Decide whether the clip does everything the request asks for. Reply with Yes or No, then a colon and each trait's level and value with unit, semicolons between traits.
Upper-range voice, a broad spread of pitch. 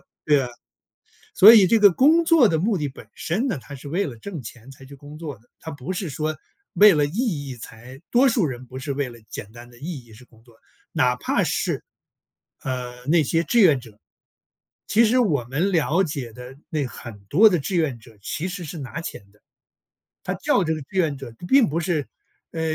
No: medium, 150 Hz; wide, 6.3 semitones